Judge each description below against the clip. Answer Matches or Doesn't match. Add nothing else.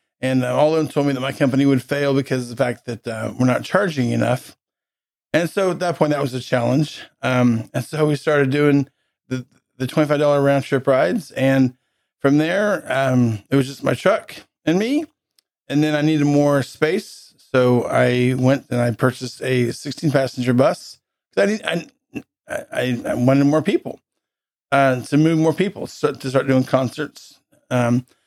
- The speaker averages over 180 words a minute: Matches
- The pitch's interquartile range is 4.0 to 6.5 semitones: Doesn't match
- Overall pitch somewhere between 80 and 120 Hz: Doesn't match